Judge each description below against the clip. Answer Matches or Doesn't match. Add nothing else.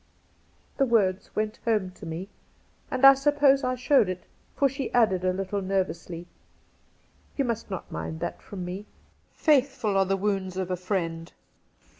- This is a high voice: Matches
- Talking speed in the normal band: Matches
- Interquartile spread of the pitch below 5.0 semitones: Doesn't match